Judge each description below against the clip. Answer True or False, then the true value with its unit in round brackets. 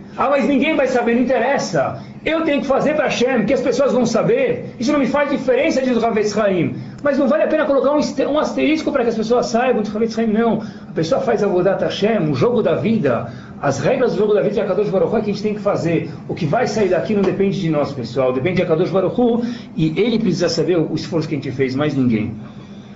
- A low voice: False (220 Hz)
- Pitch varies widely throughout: True (6.6 semitones)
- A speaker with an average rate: False (240 wpm)